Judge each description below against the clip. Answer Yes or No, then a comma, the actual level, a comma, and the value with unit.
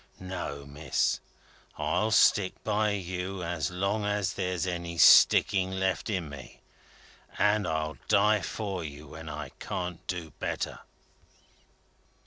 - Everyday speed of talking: No, slow, 120 wpm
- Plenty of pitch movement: No, average, 3.8 semitones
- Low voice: Yes, very low, 90 Hz